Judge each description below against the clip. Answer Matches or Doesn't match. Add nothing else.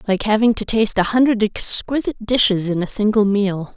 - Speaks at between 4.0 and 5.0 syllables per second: Doesn't match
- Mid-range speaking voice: Doesn't match